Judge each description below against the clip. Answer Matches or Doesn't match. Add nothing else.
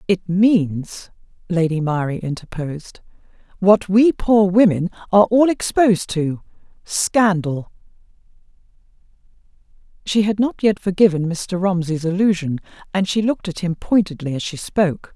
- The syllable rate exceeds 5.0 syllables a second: Doesn't match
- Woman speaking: Matches